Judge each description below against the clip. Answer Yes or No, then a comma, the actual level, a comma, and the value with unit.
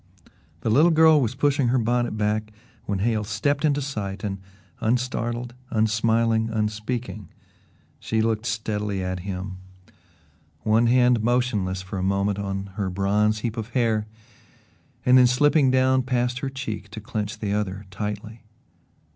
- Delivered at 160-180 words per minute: No, average, 145 wpm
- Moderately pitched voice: No, low, 110 Hz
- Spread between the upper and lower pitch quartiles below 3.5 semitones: Yes, average, 3.0 semitones